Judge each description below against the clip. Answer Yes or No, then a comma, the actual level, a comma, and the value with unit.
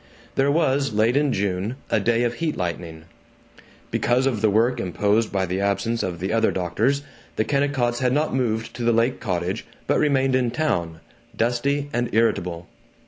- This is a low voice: Yes, low, 115 Hz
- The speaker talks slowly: No, average, 175 wpm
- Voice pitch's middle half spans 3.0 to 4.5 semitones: No, average, 5.1 semitones